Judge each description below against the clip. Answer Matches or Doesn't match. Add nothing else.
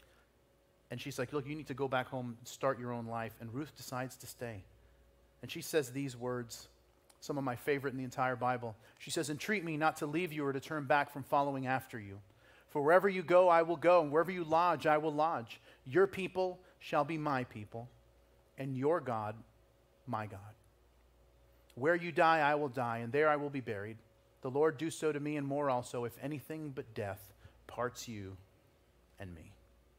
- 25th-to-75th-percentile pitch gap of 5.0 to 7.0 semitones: Matches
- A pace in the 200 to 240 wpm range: Matches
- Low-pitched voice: Matches